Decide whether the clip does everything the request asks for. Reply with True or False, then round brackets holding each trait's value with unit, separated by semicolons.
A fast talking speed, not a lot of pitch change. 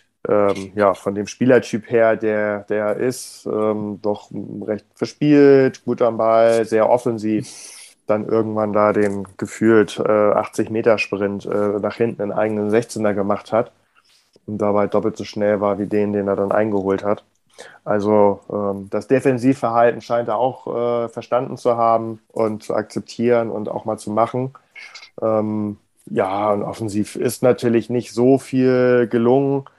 False (150 wpm; 2.3 semitones)